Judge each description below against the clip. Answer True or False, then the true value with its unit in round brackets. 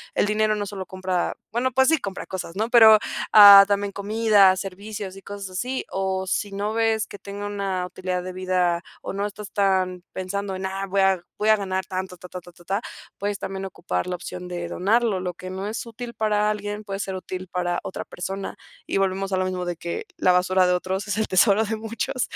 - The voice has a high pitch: True (195 Hz)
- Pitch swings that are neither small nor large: False (2.1 semitones)